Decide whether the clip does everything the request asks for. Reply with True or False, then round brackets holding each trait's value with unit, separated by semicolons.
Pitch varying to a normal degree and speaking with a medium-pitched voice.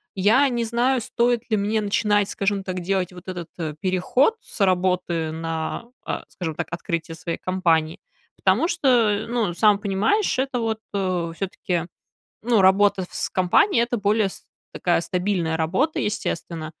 False (4.4 semitones; 195 Hz)